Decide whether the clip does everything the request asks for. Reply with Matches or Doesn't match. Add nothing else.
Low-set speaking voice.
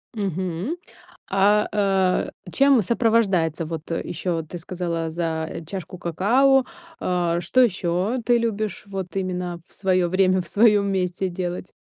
Doesn't match